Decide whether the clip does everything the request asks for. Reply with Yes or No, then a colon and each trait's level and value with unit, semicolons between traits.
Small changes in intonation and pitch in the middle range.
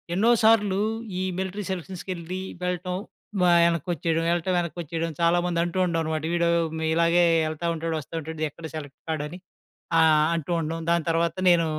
Yes: narrow, 1.7 semitones; medium, 170 Hz